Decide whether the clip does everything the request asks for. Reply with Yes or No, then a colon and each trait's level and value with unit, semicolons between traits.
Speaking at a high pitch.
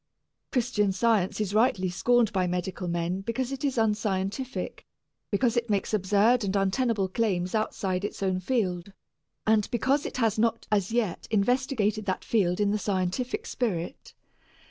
Yes: high, 210 Hz